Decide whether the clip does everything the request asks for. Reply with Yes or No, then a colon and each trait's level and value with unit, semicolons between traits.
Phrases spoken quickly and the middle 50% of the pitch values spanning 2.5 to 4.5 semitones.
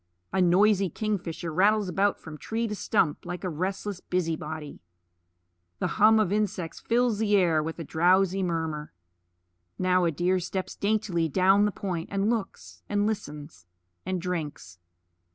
No: average, 155 wpm; average, 3.7 semitones